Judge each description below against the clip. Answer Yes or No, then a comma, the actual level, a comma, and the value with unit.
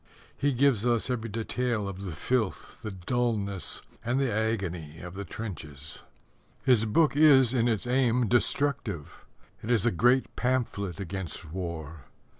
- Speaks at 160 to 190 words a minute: No, average, 145 wpm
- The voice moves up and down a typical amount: Yes, average, 4.8 semitones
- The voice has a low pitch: Yes, low, 110 Hz